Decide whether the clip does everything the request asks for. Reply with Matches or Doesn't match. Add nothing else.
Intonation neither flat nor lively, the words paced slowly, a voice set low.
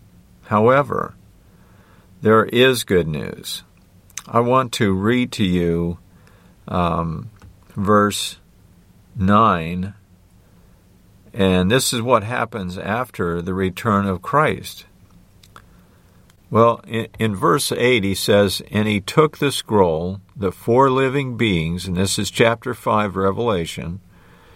Matches